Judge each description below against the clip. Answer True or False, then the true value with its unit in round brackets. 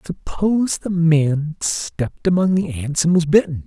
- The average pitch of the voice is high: False (165 Hz)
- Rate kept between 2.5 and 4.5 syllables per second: True (4.3 syllables/s)